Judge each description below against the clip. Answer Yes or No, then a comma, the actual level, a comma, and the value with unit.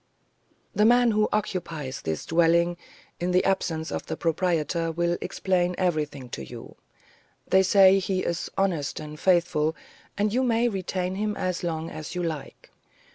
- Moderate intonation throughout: Yes, average, 3.2 semitones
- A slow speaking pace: No, average, 160 wpm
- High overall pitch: No, medium, 175 Hz